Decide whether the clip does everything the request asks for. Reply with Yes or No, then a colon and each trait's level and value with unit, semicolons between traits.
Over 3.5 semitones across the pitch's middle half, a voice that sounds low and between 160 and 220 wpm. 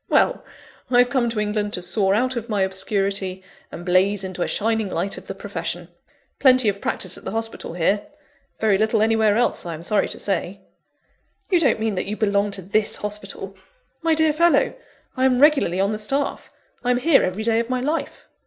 No: average, 4.0 semitones; high, 210 Hz; average, 200 wpm